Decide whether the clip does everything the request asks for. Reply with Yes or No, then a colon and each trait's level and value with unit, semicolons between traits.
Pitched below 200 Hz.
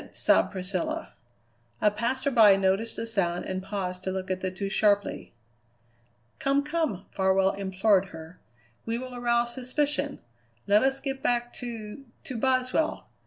No: high, 215 Hz